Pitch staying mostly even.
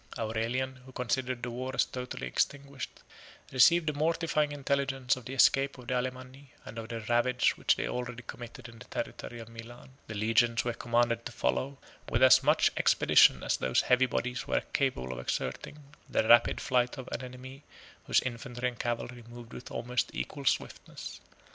Yes: narrow, 1.9 semitones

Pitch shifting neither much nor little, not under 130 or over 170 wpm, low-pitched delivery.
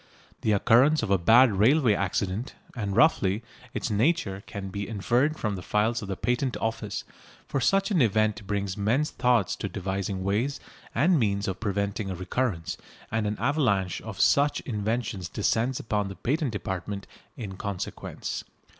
Yes: average, 3.9 semitones; average, 160 wpm; low, 105 Hz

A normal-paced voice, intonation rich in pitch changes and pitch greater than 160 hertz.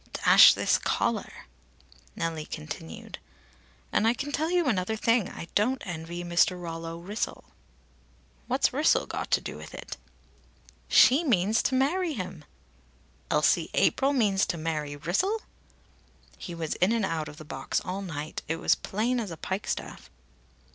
Yes: average, 155 wpm; wide, 7.1 semitones; high, 190 Hz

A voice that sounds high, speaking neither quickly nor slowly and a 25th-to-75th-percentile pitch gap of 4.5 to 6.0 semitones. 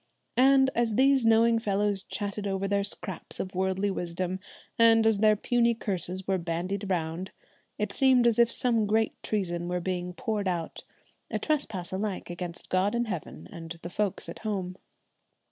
No: high, 200 Hz; average, 165 wpm; average, 3.8 semitones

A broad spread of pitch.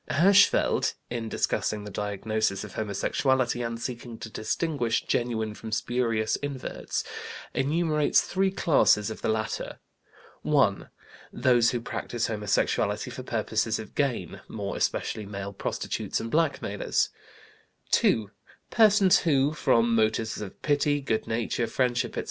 No: average, 4.5 semitones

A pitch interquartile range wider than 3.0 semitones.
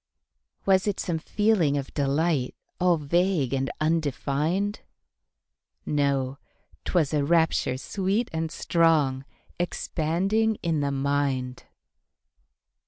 Yes: average, 4.2 semitones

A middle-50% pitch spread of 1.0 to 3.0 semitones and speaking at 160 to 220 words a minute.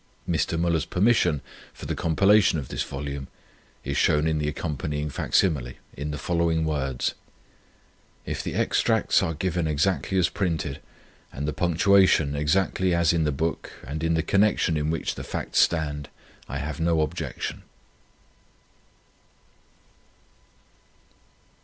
No: average, 2.7 semitones; average, 140 wpm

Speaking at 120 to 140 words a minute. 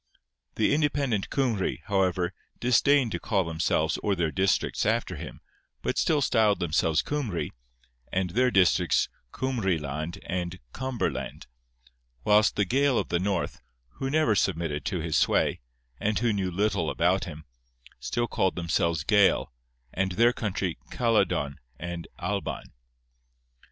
Yes: slow, 135 wpm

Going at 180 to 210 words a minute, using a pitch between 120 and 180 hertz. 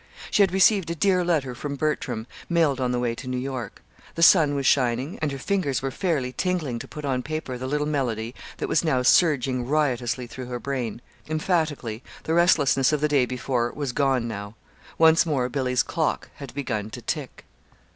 Yes: average, 195 wpm; low, 135 Hz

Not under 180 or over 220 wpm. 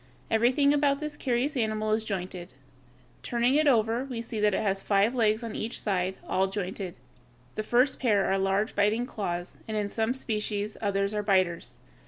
Yes: average, 190 wpm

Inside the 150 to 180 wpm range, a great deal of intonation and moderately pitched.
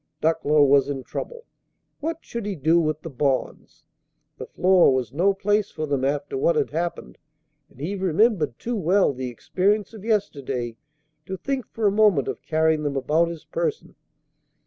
Yes: average, 170 wpm; wide, 6.5 semitones; medium, 170 Hz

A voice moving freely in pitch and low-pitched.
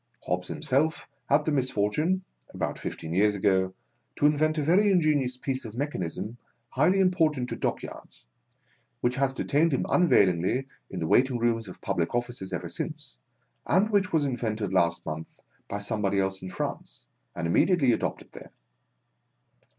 Yes: wide, 7.9 semitones; low, 125 Hz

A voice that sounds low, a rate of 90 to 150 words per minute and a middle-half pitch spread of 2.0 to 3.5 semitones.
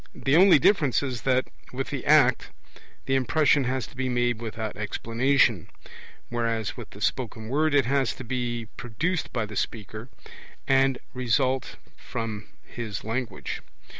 Yes: low, 125 Hz; average, 145 wpm; average, 2.9 semitones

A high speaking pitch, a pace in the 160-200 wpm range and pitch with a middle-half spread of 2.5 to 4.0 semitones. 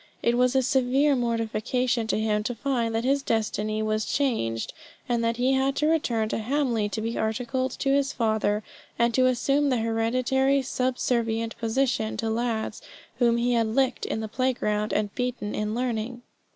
Yes: high, 235 Hz; average, 180 wpm; average, 2.8 semitones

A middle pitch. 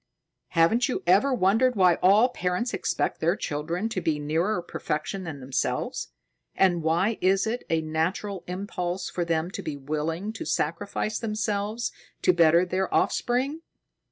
Yes: medium, 180 Hz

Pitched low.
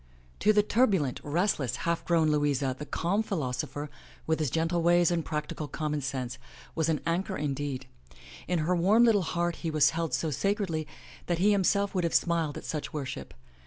No: medium, 165 Hz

